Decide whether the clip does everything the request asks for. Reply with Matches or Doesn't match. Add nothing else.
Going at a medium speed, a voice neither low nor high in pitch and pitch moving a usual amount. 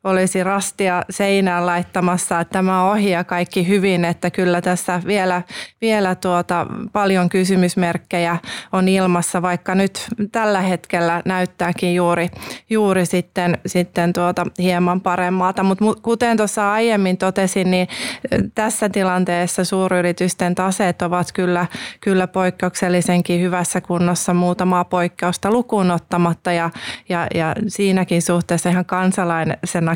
Doesn't match